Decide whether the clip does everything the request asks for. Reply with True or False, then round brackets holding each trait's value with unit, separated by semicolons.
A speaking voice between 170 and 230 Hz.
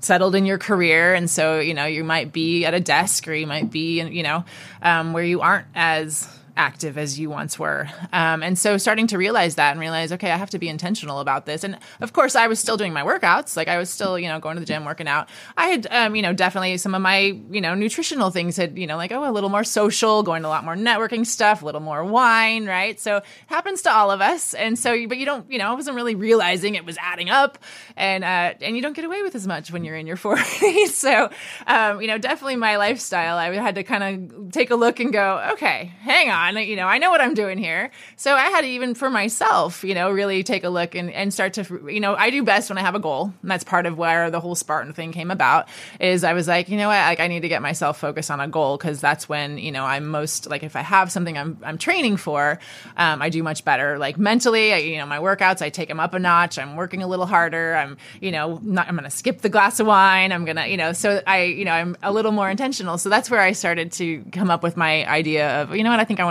True (185 Hz)